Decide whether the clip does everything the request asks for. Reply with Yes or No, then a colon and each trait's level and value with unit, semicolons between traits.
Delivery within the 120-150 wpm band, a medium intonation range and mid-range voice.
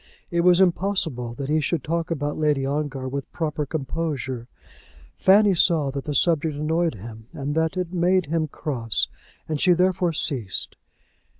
No: average, 160 wpm; average, 3.8 semitones; medium, 155 Hz